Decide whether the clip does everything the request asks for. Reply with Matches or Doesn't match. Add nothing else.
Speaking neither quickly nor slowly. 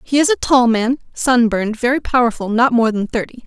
Doesn't match